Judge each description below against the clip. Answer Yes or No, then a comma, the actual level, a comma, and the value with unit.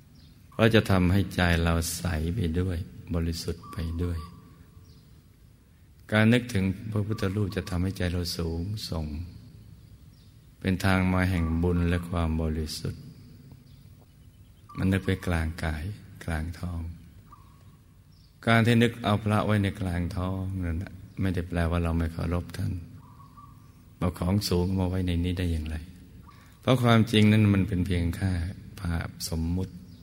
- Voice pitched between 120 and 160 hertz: No, very low, 90 Hz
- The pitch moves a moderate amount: Yes, average, 3.4 semitones